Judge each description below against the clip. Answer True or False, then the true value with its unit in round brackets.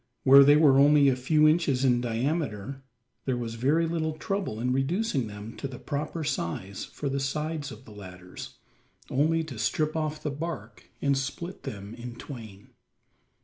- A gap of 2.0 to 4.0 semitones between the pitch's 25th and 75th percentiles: False (4.7 semitones)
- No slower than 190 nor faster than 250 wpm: False (170 wpm)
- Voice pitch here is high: False (135 Hz)